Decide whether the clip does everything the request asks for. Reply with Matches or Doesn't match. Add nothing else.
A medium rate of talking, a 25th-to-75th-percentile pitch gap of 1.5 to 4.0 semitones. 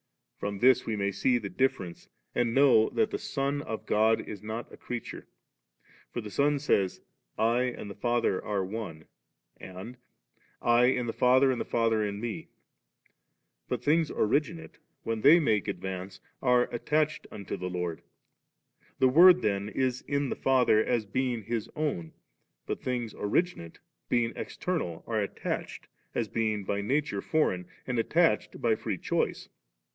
Doesn't match